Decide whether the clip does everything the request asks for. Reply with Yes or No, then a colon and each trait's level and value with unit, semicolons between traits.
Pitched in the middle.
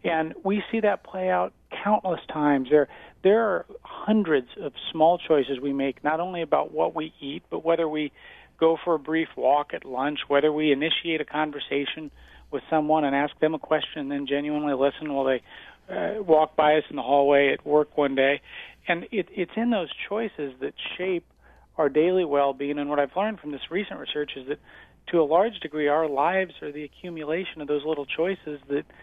Yes: medium, 155 Hz